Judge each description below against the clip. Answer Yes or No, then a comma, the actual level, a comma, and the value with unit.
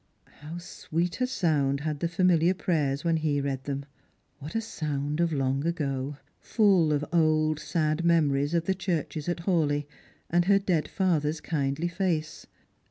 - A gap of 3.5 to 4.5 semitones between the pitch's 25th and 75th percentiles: No, average, 3.0 semitones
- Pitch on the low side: No, medium, 155 Hz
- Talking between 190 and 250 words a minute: No, average, 165 wpm